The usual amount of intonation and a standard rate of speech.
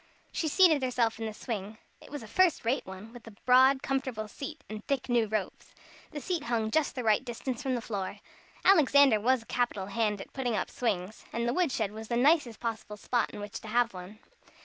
No: average, 3.7 semitones; fast, 215 wpm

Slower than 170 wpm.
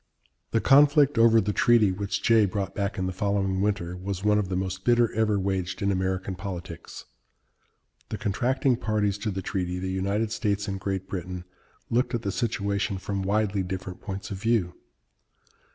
No: average, 175 wpm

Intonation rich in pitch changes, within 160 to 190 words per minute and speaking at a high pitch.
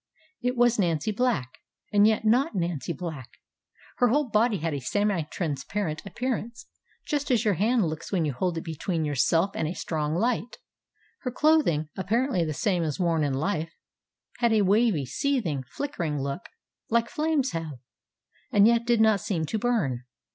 Yes: wide, 6.9 semitones; average, 170 wpm; high, 195 Hz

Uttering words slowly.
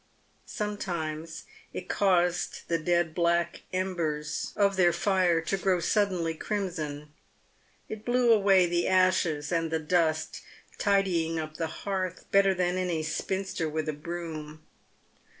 Yes: slow, 130 wpm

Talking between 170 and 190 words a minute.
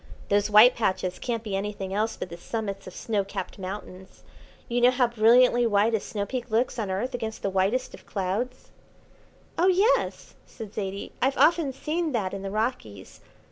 Yes: average, 180 wpm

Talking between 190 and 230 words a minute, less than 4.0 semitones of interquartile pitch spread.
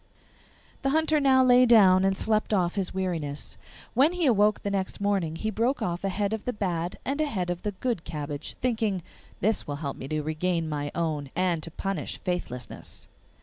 No: average, 195 wpm; average, 5.1 semitones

